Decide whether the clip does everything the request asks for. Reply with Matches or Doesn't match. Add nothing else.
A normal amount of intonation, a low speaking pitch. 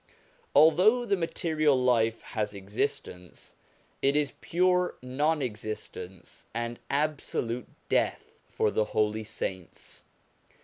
Doesn't match